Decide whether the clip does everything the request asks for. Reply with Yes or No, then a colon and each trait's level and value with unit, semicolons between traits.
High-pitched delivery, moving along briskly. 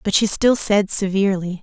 No: high, 200 Hz; average, 185 wpm